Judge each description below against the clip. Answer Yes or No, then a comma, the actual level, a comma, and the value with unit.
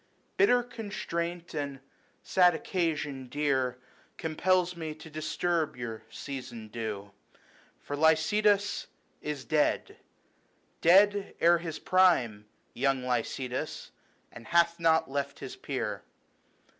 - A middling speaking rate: No, slow, 105 wpm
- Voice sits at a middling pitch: Yes, medium, 155 Hz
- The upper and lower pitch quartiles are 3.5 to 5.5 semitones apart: Yes, average, 4.8 semitones